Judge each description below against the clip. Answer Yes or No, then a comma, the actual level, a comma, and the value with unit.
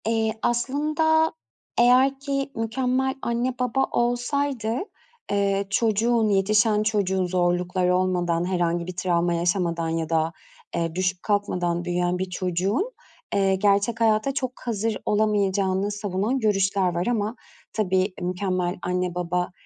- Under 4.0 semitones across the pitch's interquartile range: No, average, 4.4 semitones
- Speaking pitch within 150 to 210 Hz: Yes, high, 200 Hz